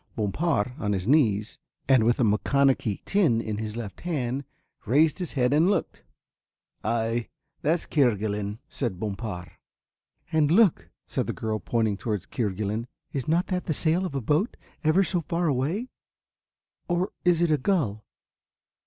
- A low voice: Yes, low, 125 Hz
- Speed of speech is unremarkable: Yes, average, 155 wpm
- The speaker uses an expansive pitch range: Yes, wide, 7.1 semitones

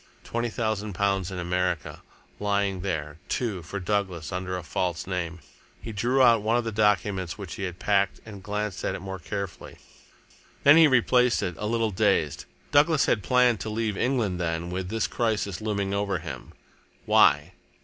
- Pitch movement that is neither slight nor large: Yes, average, 3.5 semitones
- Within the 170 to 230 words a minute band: Yes, average, 175 wpm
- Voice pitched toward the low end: Yes, low, 100 Hz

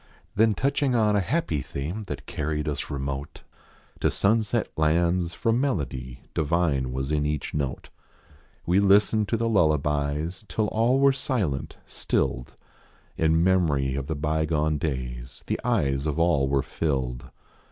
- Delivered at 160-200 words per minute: No, average, 140 wpm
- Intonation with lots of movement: Yes, wide, 6.6 semitones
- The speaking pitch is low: Yes, very low, 80 Hz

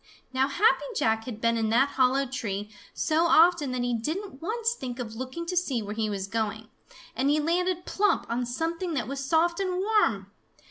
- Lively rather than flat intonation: Yes, wide, 6.9 semitones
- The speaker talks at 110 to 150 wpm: No, average, 195 wpm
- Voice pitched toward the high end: Yes, very high, 270 Hz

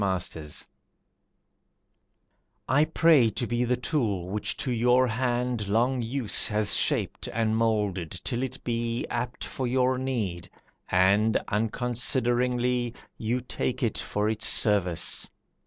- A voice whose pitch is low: Yes, low, 120 Hz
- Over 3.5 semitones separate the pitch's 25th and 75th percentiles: No, average, 3.1 semitones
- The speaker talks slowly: Yes, slow, 125 wpm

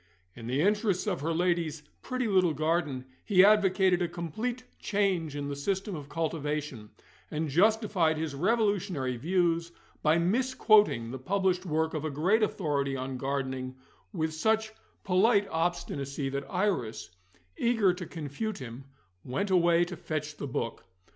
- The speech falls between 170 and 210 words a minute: No, average, 145 wpm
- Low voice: No, medium, 170 Hz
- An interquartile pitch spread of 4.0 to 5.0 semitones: No, wide, 5.5 semitones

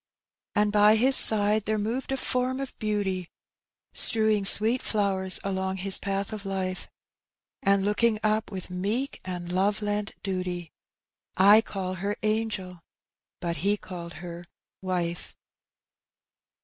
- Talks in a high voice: Yes, high, 200 Hz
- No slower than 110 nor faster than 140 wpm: Yes, slow, 135 wpm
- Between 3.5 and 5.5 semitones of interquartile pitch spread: No, narrow, 2.6 semitones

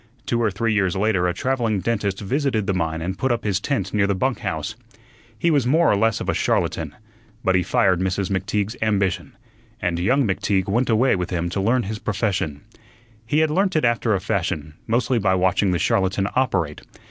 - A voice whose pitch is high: No, low, 100 Hz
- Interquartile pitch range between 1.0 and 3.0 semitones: No, average, 4.0 semitones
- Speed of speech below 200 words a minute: No, fast, 205 wpm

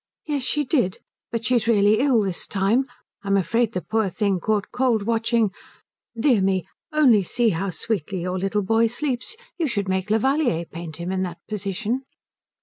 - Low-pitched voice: No, high, 215 Hz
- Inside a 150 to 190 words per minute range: Yes, average, 170 wpm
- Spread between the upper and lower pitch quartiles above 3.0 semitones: Yes, average, 4.1 semitones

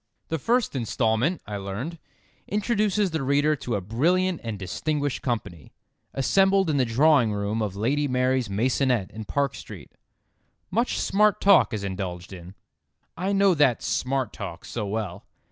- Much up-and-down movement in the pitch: Yes, wide, 7.7 semitones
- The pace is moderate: Yes, average, 150 wpm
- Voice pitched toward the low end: Yes, low, 130 Hz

